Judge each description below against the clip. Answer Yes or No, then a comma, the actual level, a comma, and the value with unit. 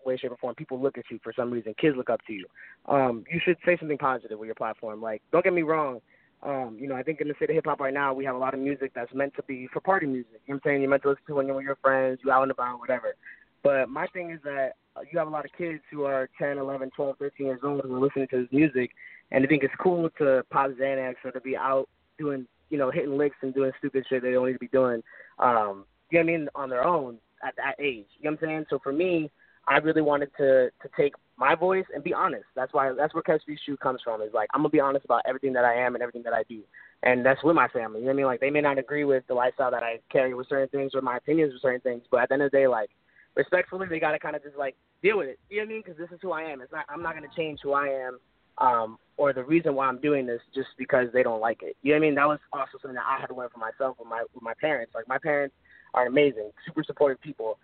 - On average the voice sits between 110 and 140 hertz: Yes, low, 135 Hz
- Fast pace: Yes, fast, 305 wpm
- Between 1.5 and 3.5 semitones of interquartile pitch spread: Yes, average, 2.8 semitones